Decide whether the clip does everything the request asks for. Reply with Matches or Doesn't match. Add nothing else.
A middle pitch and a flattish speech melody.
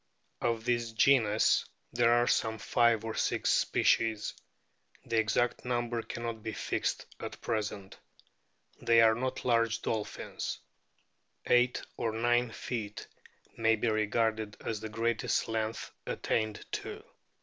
Doesn't match